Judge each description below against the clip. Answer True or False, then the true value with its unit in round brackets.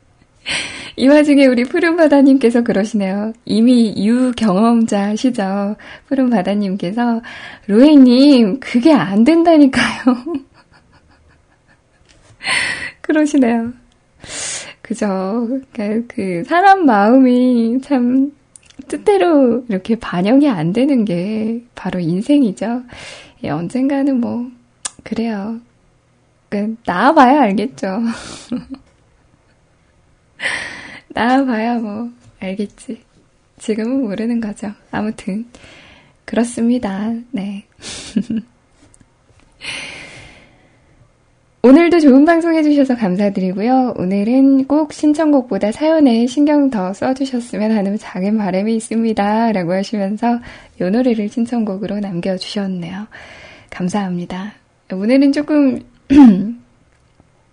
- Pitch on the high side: True (235 Hz)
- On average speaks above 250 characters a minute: False (210 characters per minute)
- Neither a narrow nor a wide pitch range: True (4.5 semitones)